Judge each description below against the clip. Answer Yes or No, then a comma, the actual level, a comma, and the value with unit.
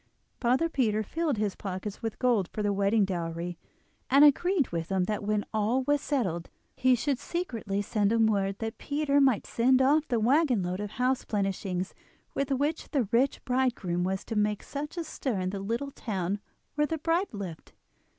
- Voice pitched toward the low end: No, high, 225 Hz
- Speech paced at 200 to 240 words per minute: No, average, 185 wpm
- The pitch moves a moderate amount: No, wide, 5.8 semitones